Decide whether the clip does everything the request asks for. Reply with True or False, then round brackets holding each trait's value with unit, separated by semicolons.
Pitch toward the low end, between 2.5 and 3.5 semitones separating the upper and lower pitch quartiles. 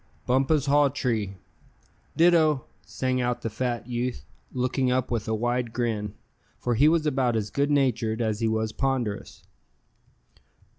True (125 Hz; 3.2 semitones)